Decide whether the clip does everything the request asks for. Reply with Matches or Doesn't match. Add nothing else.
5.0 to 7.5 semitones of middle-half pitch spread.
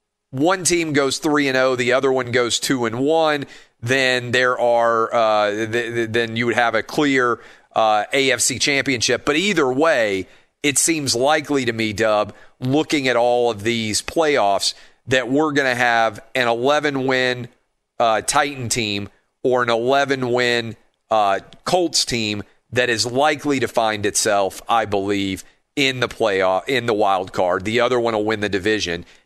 Doesn't match